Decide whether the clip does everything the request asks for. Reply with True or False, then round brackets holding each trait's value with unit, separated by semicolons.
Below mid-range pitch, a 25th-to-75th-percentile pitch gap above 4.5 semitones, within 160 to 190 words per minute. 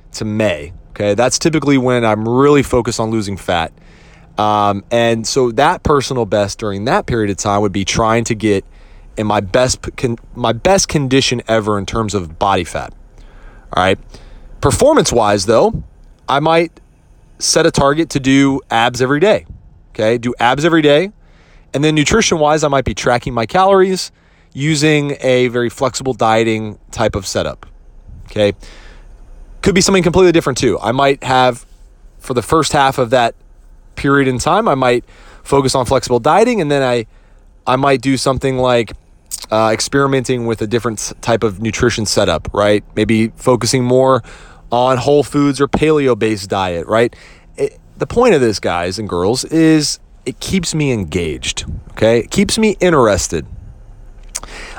True (125 Hz; 4.9 semitones; 165 wpm)